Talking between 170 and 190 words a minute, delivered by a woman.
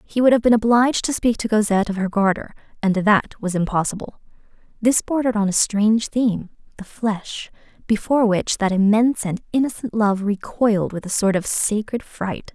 Yes: average, 180 wpm; female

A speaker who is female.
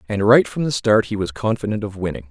No: male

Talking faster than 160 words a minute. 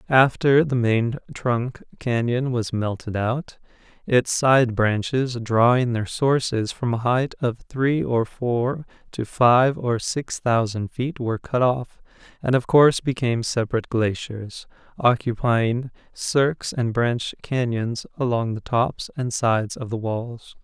No: average, 145 wpm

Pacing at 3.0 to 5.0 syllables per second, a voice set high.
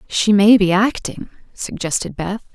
Yes: 4.2 syllables/s; high, 200 Hz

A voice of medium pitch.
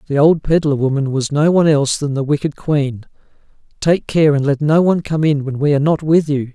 Yes: medium, 145 Hz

